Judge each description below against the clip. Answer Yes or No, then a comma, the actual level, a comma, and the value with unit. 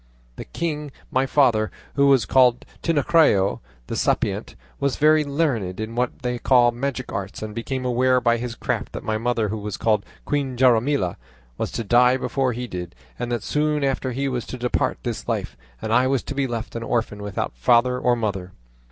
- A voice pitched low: Yes, low, 125 Hz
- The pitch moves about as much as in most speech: Yes, average, 3.3 semitones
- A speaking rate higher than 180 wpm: Yes, average, 195 wpm